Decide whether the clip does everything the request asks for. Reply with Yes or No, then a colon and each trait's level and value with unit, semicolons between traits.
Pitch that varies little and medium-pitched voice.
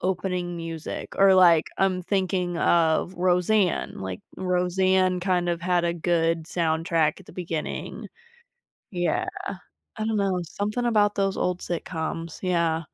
Yes: narrow, 2.1 semitones; medium, 180 Hz